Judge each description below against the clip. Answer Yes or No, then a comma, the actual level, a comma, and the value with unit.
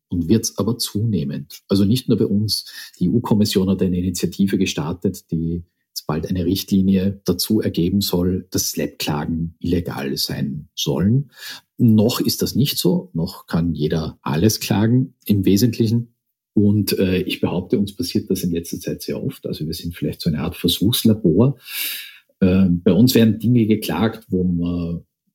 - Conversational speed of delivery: Yes, average, 165 wpm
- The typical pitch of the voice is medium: No, low, 100 Hz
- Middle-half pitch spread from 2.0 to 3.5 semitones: No, average, 4.1 semitones